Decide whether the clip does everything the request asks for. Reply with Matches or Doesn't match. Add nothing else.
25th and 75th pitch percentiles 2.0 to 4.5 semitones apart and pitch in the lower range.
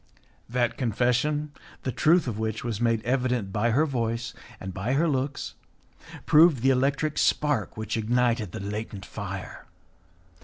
Matches